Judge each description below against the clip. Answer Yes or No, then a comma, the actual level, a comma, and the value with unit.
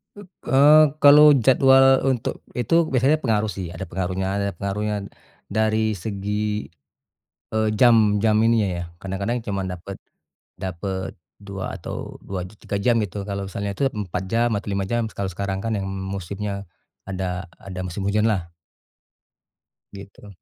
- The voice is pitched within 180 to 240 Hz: No, low, 100 Hz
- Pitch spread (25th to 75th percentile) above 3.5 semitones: No, average, 2.8 semitones